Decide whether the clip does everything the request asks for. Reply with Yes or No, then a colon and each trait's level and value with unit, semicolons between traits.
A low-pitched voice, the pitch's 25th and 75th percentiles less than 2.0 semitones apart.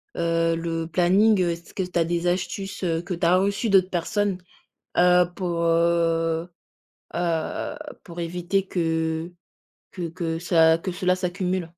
No: medium, 175 Hz; narrow, 1.6 semitones